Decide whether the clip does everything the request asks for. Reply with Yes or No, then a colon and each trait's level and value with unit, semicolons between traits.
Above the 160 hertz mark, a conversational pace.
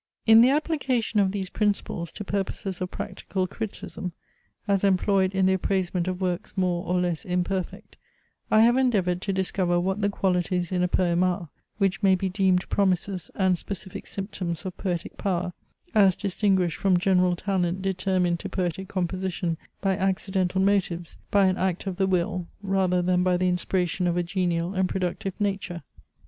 Yes: medium, 185 Hz; average, 170 wpm